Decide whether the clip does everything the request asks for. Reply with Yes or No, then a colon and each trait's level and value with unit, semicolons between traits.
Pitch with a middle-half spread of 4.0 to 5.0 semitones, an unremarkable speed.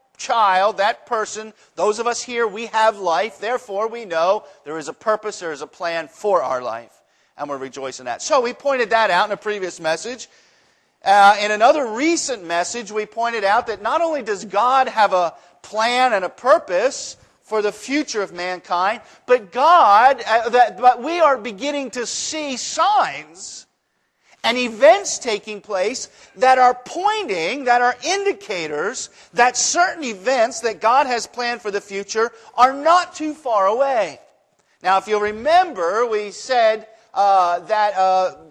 Yes: average, 4.4 semitones; average, 160 wpm